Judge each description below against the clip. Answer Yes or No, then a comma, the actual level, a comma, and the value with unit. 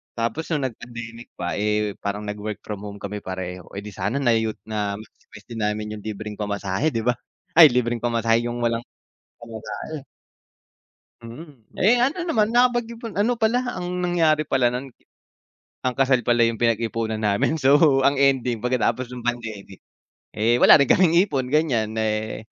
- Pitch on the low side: Yes, low, 120 Hz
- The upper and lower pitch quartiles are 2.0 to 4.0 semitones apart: No, average, 5.0 semitones